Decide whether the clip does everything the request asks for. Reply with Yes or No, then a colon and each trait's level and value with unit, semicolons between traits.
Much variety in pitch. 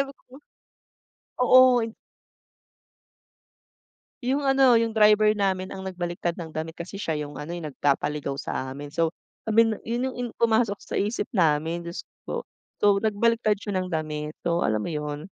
Yes: wide, 6.3 semitones